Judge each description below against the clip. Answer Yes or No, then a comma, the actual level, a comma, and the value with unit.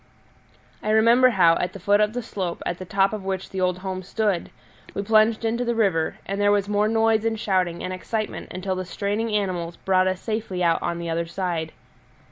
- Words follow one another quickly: Yes, fast, 215 wpm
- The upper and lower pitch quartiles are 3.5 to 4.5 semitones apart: No, average, 3.1 semitones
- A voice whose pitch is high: Yes, high, 195 Hz